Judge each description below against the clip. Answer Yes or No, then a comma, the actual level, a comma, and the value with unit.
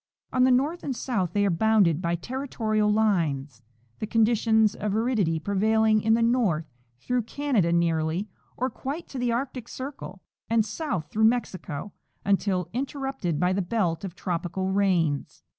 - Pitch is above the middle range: Yes, high, 215 Hz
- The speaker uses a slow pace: No, average, 155 wpm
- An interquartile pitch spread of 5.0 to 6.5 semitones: Yes, average, 5.3 semitones